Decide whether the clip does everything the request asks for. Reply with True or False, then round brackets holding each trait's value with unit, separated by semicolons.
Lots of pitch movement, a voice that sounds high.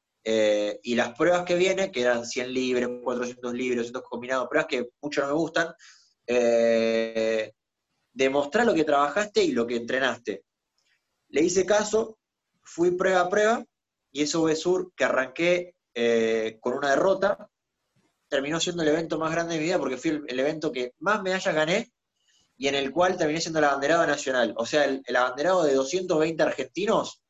False (6.3 semitones; 150 Hz)